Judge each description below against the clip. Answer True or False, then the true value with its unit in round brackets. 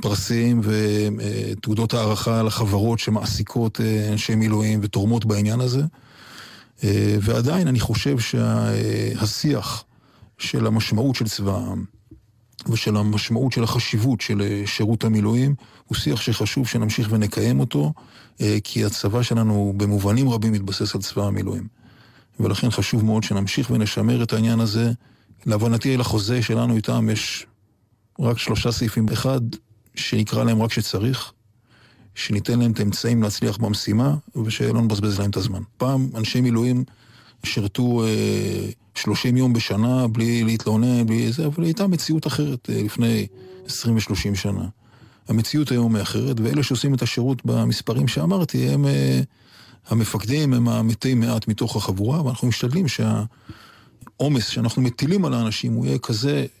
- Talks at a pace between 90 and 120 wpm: False (130 wpm)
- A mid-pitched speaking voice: False (115 Hz)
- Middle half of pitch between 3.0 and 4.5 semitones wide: False (2.4 semitones)